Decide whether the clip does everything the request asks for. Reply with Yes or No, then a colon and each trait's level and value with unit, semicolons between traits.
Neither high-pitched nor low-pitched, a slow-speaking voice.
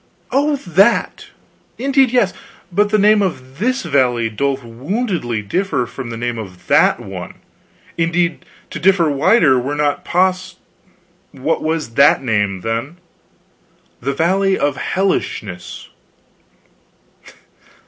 Yes: medium, 160 Hz; slow, 120 wpm